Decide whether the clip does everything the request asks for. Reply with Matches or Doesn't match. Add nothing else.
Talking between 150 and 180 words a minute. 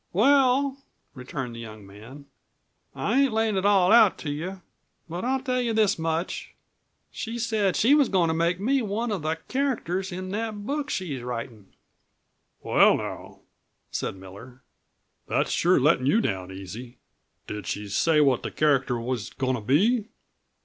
Matches